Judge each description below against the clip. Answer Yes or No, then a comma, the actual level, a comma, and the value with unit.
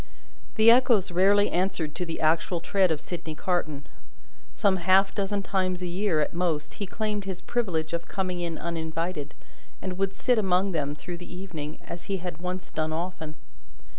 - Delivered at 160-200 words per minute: Yes, average, 175 wpm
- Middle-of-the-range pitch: Yes, medium, 180 Hz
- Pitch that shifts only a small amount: No, average, 3.0 semitones